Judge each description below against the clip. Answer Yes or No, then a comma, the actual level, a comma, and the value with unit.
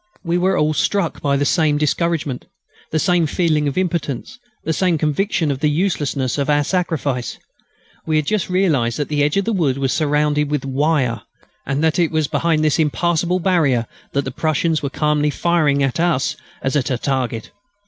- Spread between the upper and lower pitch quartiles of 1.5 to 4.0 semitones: Yes, average, 3.2 semitones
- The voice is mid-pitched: Yes, medium, 150 Hz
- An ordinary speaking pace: Yes, average, 190 wpm